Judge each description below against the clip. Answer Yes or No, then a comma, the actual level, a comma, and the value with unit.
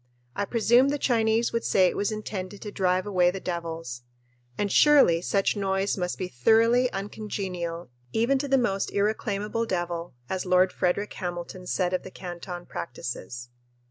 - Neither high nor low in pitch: No, high, 195 Hz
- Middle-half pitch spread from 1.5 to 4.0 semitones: Yes, average, 3.6 semitones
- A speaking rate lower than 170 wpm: Yes, average, 160 wpm